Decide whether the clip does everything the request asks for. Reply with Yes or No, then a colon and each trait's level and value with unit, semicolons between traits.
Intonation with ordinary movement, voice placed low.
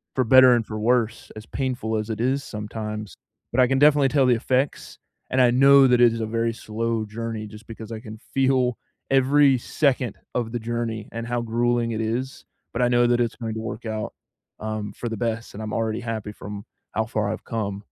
No: narrow, 2.3 semitones; low, 115 Hz